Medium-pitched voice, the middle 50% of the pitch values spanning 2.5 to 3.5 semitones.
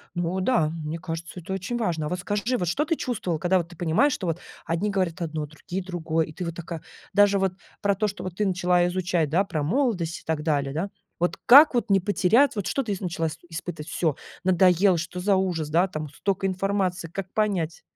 Yes: medium, 180 Hz; average, 3.2 semitones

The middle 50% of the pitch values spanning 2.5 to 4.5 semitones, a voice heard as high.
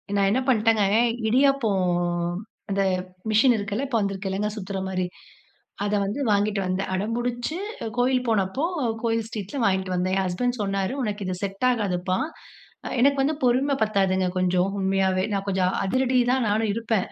Yes: average, 4.0 semitones; high, 205 Hz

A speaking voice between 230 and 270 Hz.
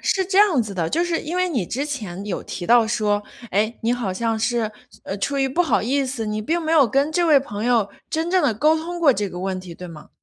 Yes: high, 240 Hz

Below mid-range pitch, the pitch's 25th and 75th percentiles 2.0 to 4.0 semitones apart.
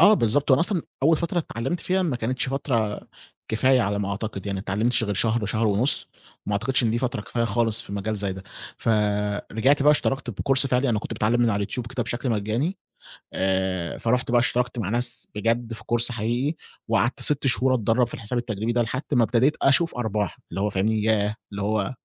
Yes: low, 115 Hz; average, 3.5 semitones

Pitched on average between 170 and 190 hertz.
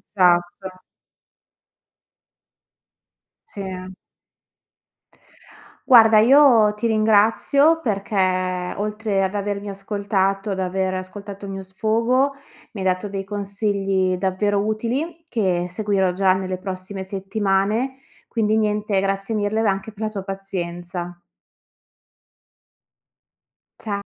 No: high, 200 Hz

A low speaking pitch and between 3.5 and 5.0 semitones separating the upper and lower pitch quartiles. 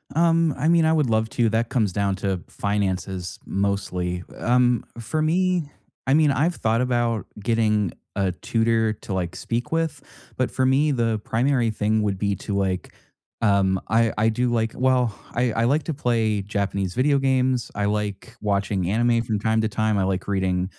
Yes: low, 110 Hz; average, 4.0 semitones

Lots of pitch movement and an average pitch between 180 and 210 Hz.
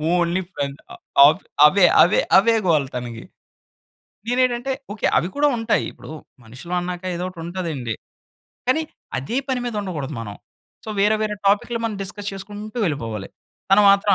Yes: wide, 6.1 semitones; high, 190 Hz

